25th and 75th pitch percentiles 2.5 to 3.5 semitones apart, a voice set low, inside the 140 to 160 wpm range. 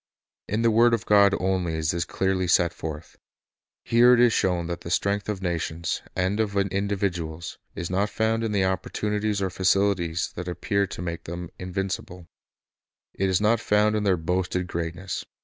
No: average, 2.9 semitones; very low, 95 Hz; average, 175 wpm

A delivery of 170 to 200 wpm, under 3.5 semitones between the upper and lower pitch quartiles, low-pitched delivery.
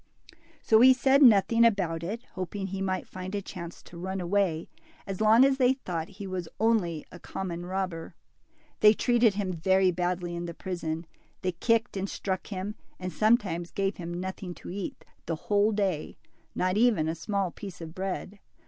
No: average, 180 wpm; average, 3.1 semitones; high, 190 Hz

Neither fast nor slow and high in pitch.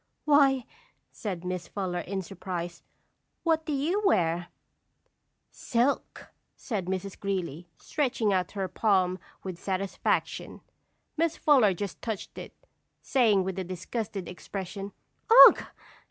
No: slow, 115 wpm; high, 195 Hz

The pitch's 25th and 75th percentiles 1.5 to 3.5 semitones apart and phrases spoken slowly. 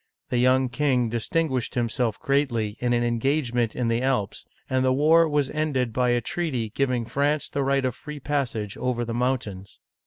No: average, 2.9 semitones; average, 185 wpm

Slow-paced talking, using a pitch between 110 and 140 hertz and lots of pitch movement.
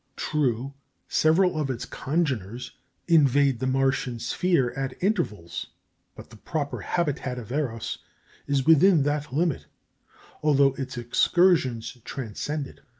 No: slow, 120 wpm; low, 135 Hz; average, 3.8 semitones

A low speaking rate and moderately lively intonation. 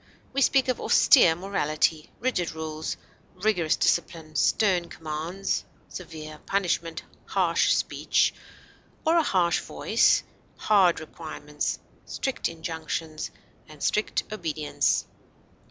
Yes: slow, 100 wpm; average, 4.0 semitones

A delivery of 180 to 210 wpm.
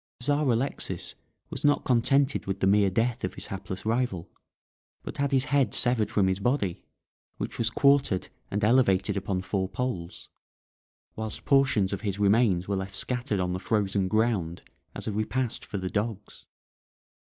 No: average, 165 wpm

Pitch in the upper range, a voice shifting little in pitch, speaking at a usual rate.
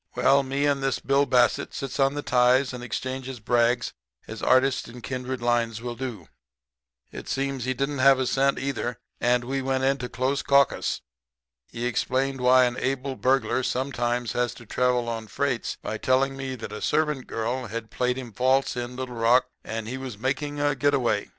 No: low, 130 Hz; narrow, 1.9 semitones; average, 190 wpm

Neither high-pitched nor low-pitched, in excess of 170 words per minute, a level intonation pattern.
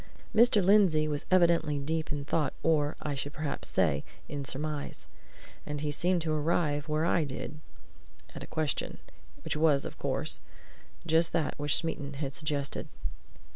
No: medium, 155 Hz; average, 155 wpm; narrow, 2.1 semitones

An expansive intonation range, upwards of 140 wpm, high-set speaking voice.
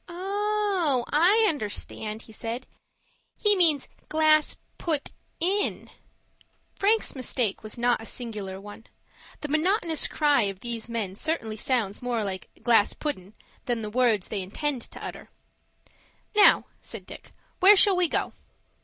No: wide, 7.8 semitones; slow, 135 wpm; very high, 255 Hz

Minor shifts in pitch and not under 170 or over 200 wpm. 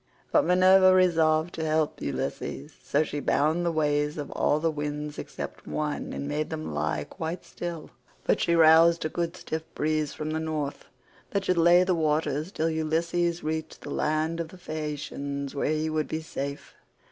Yes: narrow, 2.0 semitones; average, 180 wpm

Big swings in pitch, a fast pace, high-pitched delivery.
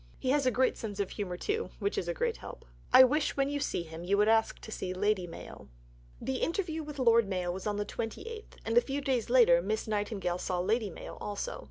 Yes: wide, 5.8 semitones; fast, 235 wpm; high, 225 Hz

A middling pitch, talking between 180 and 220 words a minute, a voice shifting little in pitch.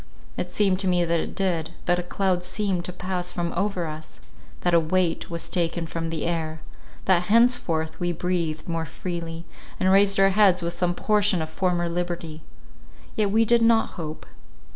Yes: medium, 175 Hz; average, 185 wpm; narrow, 2.3 semitones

